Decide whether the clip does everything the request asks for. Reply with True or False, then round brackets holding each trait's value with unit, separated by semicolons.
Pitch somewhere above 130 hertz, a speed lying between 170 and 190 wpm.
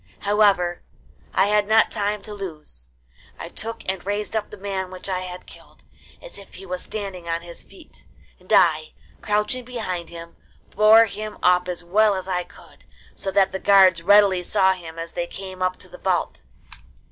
True (190 Hz; 185 wpm)